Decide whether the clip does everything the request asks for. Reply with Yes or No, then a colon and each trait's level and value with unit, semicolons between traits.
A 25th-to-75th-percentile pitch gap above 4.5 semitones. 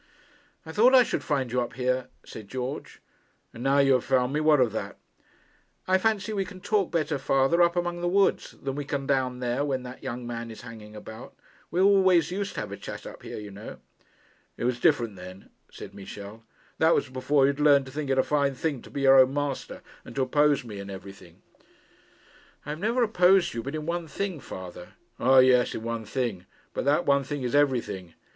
Yes: average, 5.0 semitones